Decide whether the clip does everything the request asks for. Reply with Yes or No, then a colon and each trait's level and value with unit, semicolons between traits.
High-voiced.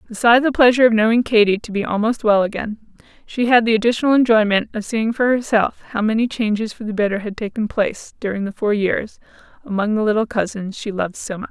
Yes: high, 220 Hz